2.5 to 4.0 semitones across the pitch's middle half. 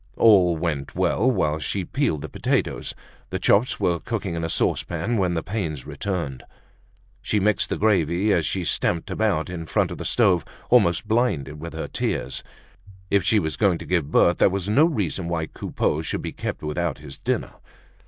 No: average, 4.6 semitones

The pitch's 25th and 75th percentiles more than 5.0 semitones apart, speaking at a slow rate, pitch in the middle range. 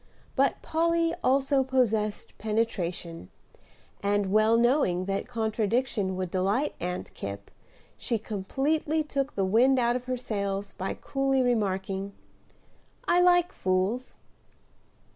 No: wide, 5.5 semitones; slow, 115 wpm; high, 225 Hz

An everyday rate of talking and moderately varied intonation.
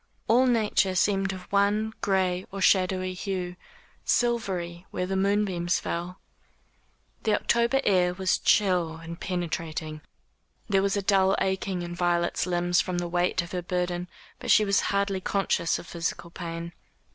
No: average, 150 wpm; narrow, 2.2 semitones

